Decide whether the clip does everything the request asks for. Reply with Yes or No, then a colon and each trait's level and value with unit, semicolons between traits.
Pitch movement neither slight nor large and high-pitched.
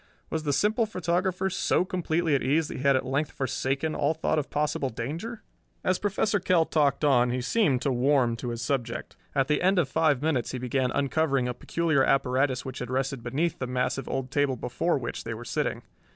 No: average, 4.1 semitones; medium, 140 Hz